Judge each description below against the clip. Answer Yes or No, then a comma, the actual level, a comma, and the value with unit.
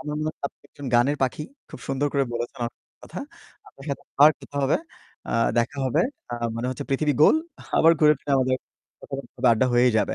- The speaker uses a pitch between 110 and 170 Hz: Yes, low, 135 Hz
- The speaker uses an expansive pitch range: No, average, 2.8 semitones